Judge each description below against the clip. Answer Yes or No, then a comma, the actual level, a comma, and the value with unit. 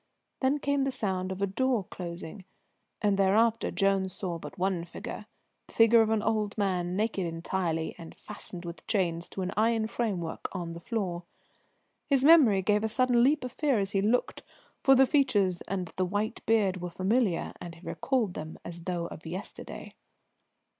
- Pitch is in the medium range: No, high, 195 Hz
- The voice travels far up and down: No, average, 4.2 semitones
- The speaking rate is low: No, average, 175 wpm